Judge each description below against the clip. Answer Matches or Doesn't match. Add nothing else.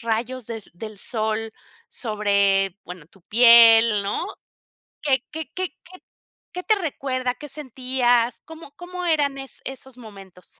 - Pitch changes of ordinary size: Matches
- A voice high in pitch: Matches